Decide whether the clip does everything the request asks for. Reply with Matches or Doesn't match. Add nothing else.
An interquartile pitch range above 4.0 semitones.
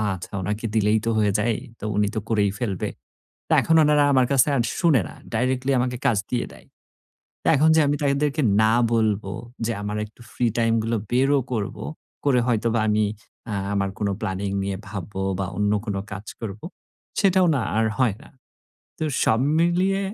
Matches